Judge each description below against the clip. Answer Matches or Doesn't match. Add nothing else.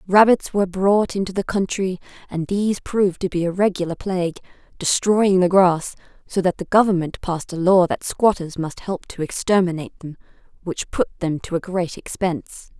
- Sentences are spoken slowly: Doesn't match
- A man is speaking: Doesn't match